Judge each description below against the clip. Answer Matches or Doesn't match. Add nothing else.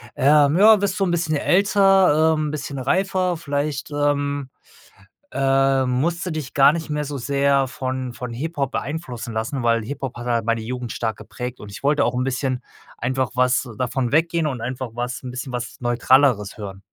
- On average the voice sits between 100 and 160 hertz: Matches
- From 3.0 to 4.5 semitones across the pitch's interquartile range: Matches